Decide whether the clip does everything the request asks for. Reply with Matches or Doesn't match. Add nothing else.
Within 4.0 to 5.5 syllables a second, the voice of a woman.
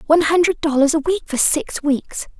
Matches